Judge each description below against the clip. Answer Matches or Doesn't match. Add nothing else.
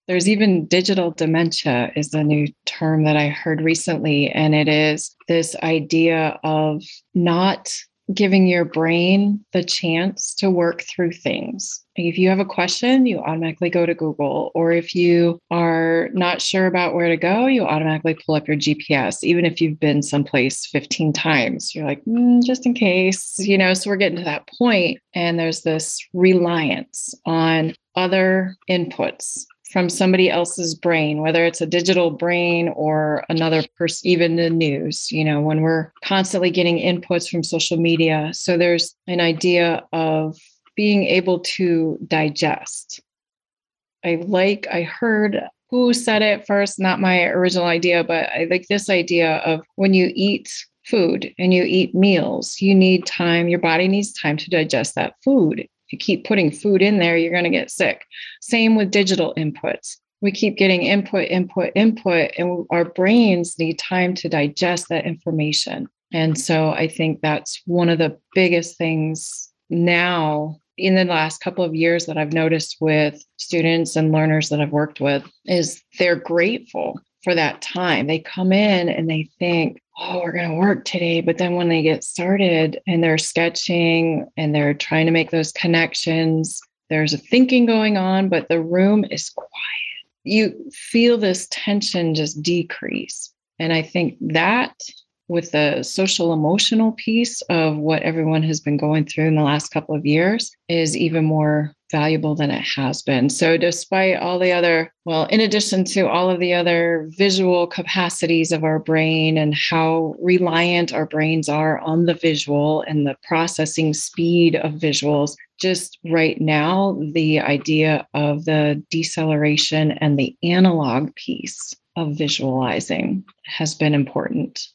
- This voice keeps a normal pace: Matches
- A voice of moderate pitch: Matches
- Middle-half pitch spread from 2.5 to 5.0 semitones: Matches